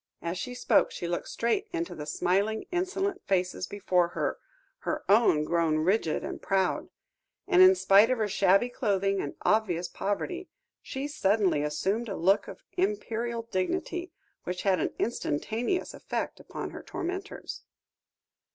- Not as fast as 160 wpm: Yes, average, 145 wpm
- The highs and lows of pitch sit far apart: Yes, wide, 7.6 semitones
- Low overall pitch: No, high, 205 Hz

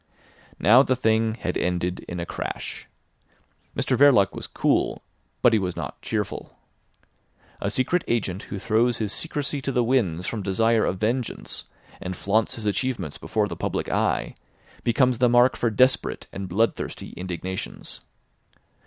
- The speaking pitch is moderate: No, low, 110 Hz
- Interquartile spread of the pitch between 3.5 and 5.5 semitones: Yes, average, 4.7 semitones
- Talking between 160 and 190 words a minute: No, average, 150 wpm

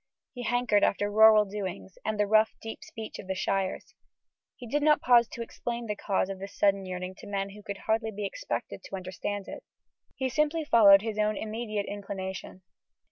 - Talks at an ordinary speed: Yes, average, 190 wpm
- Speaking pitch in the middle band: No, high, 210 Hz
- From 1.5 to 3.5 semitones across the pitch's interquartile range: Yes, average, 2.7 semitones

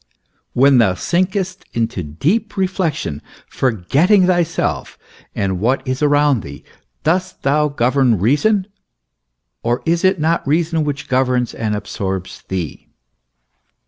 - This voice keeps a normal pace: No, slow, 115 wpm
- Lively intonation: Yes, wide, 7.1 semitones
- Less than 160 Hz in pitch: Yes, medium, 140 Hz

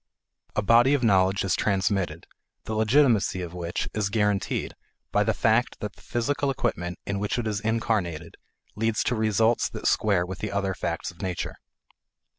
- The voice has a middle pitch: No, low, 100 Hz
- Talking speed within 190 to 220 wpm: No, average, 170 wpm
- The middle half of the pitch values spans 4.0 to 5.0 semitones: No, average, 3.3 semitones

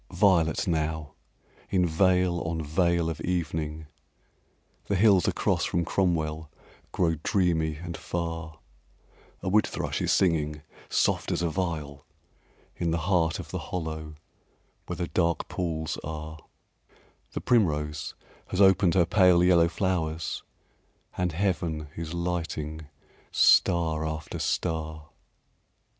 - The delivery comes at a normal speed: No, slow, 120 wpm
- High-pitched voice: No, very low, 85 Hz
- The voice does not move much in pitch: Yes, narrow, 2.2 semitones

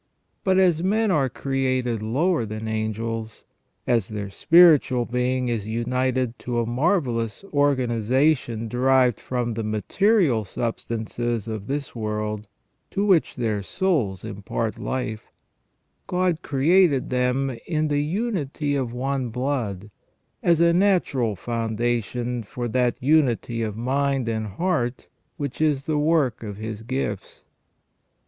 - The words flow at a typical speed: No, slow, 125 wpm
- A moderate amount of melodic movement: Yes, average, 4.5 semitones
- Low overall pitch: Yes, low, 125 Hz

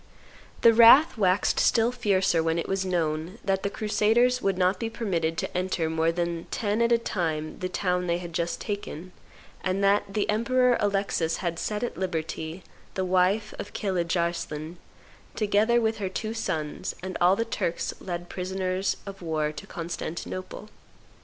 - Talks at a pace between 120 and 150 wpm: No, average, 165 wpm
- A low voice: No, medium, 185 Hz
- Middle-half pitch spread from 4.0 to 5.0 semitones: No, average, 3.6 semitones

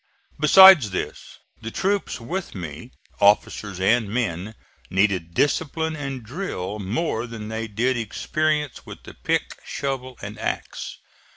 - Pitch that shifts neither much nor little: No, wide, 6.5 semitones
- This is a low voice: Yes, low, 115 Hz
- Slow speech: Yes, slow, 125 wpm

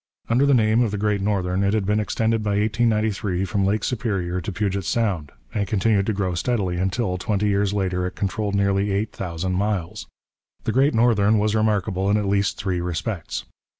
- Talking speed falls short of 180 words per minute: No, average, 190 wpm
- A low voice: Yes, low, 100 Hz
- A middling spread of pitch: No, narrow, 2.3 semitones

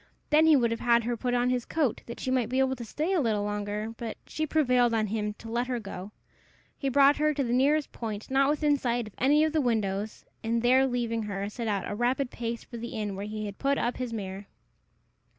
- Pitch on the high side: Yes, high, 240 Hz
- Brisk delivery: Yes, fast, 250 wpm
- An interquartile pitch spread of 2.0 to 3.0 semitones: No, average, 3.7 semitones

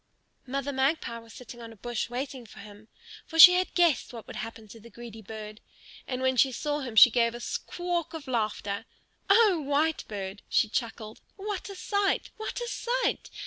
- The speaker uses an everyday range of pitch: No, wide, 6.4 semitones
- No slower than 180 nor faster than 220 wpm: Yes, average, 185 wpm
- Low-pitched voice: No, very high, 255 Hz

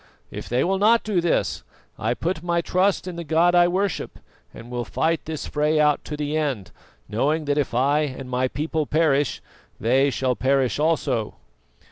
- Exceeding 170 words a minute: Yes, average, 180 wpm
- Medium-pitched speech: Yes, medium, 150 Hz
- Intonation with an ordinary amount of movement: Yes, average, 4.3 semitones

